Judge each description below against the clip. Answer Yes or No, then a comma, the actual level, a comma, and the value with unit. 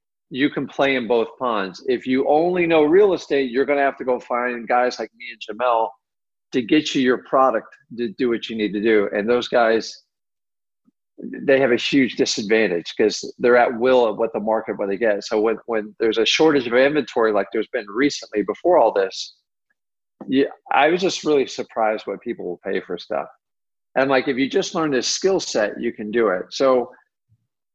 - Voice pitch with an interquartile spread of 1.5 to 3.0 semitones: No, average, 4.2 semitones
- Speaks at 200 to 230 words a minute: Yes, fast, 205 wpm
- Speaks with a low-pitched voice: Yes, low, 125 Hz